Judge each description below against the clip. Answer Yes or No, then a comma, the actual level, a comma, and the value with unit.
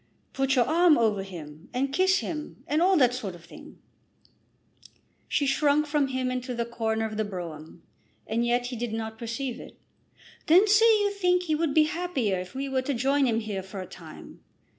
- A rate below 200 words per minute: No, fast, 205 wpm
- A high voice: Yes, very high, 255 Hz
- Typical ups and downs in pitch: No, wide, 5.7 semitones